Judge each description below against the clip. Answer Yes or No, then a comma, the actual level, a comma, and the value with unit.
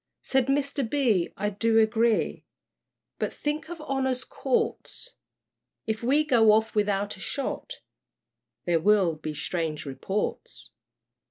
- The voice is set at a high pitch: Yes, high, 225 Hz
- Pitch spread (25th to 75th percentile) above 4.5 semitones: Yes, wide, 5.6 semitones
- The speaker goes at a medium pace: No, slow, 120 wpm